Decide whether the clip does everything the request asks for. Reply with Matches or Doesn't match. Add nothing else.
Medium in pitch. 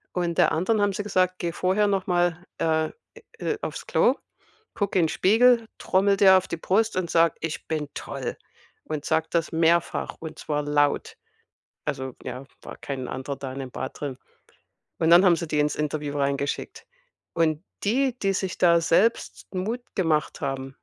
Matches